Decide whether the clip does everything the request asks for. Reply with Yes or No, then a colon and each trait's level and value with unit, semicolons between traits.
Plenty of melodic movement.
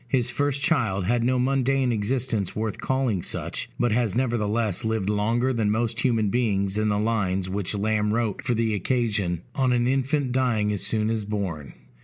No: average, 3.2 semitones